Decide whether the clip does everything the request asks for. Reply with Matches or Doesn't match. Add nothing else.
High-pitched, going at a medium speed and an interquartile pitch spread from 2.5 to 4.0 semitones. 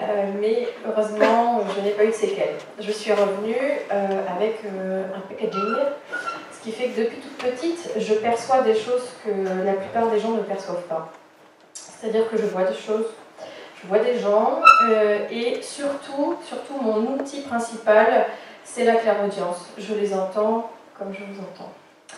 Matches